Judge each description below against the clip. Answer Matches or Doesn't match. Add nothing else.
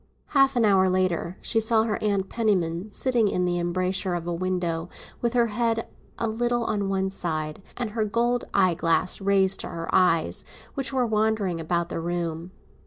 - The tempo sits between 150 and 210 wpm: Matches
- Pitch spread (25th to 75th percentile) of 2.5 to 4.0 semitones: Doesn't match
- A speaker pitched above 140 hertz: Matches